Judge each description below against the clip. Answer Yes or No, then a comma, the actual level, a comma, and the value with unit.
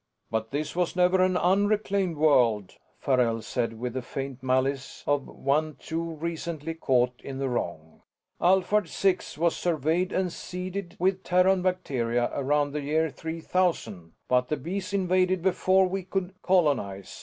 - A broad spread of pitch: Yes, wide, 5.9 semitones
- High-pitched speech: No, medium, 160 Hz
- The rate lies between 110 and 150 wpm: Yes, average, 145 wpm